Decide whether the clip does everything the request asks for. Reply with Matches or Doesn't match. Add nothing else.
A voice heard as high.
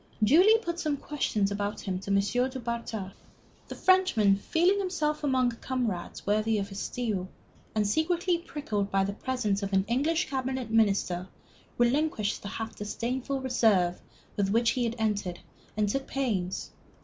Matches